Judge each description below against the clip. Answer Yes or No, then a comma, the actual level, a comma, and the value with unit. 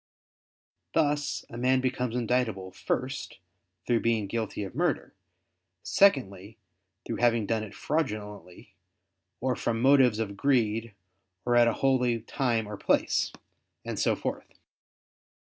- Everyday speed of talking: No, slow, 125 wpm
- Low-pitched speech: Yes, low, 115 Hz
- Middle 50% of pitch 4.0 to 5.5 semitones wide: No, average, 3.2 semitones